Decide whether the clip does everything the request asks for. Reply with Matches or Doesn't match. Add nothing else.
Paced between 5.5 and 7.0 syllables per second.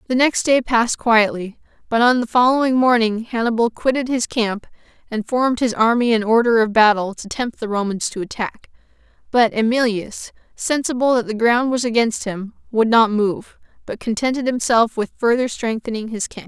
Doesn't match